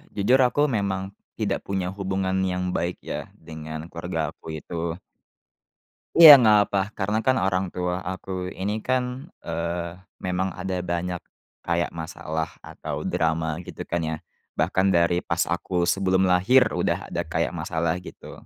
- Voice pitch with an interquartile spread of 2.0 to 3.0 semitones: Yes, narrow, 2.4 semitones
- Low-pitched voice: Yes, very low, 90 Hz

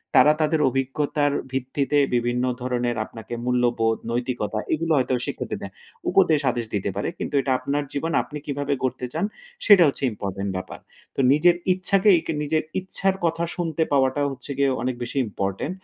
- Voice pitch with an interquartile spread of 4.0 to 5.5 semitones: Yes, average, 4.5 semitones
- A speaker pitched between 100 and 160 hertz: Yes, low, 135 Hz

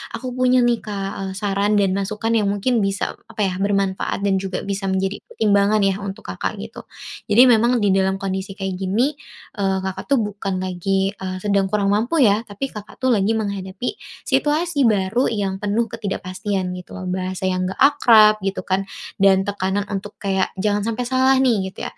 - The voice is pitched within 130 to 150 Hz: No, high, 200 Hz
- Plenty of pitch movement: No, narrow, 2.5 semitones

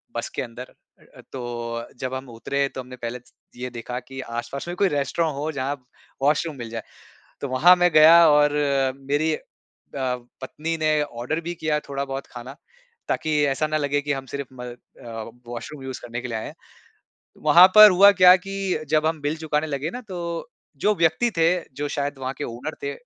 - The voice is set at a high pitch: No, medium, 140 Hz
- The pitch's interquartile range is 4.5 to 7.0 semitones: No, average, 3.7 semitones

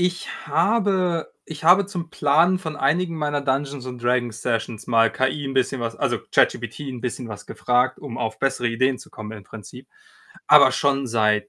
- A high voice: No, low, 135 Hz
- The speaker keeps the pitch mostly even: No, average, 5.3 semitones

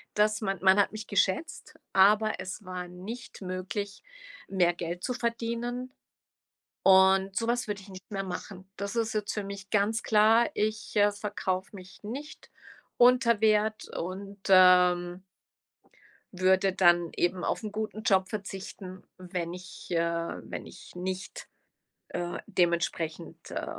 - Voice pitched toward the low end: No, high, 195 Hz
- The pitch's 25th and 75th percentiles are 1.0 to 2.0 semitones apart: No, average, 2.8 semitones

